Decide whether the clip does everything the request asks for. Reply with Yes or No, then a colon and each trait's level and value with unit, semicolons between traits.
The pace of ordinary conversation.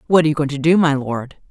No: fast, 320 wpm